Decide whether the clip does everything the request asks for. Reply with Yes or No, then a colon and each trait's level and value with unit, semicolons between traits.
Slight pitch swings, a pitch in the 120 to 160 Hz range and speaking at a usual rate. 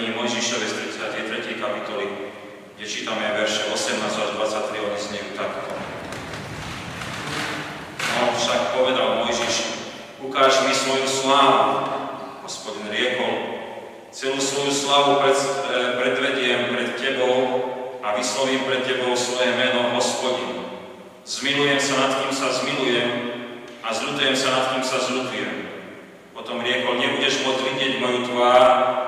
Yes: narrow, 1.9 semitones; low, 125 Hz; average, 120 wpm